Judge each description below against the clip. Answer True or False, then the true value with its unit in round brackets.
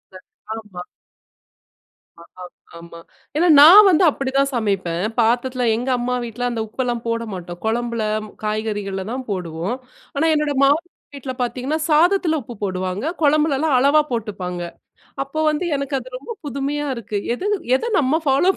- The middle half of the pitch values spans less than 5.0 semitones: False (5.5 semitones)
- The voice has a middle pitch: False (250 Hz)